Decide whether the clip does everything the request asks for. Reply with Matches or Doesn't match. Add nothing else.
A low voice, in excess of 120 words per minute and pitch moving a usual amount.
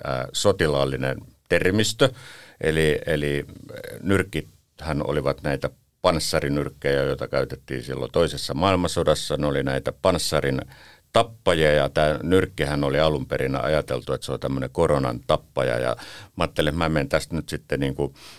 Matches